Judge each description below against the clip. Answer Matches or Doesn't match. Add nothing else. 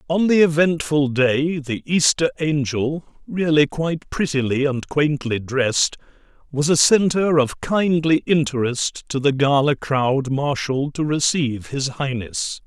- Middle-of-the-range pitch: Matches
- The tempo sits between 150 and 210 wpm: Doesn't match